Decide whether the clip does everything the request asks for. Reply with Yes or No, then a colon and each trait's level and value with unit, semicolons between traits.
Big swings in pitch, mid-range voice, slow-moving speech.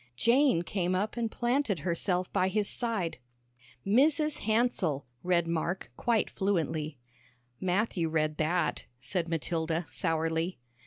No: average, 5.0 semitones; medium, 180 Hz; slow, 115 wpm